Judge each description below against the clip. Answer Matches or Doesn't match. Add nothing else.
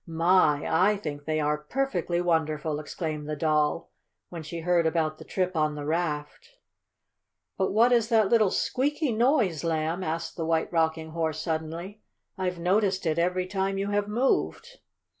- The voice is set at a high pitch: Doesn't match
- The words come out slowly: Doesn't match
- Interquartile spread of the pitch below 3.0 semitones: Doesn't match